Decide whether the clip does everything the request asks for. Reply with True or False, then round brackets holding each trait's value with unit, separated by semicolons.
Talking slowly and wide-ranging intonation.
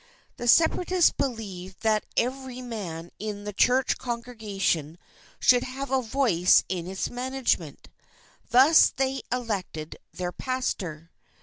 True (115 wpm; 5.7 semitones)